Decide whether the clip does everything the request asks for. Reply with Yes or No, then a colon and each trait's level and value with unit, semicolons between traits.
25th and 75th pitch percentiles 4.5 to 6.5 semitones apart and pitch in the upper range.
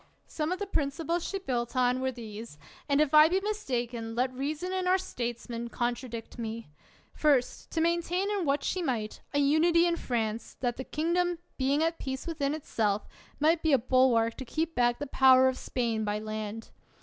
Yes: wide, 5.5 semitones; very high, 265 Hz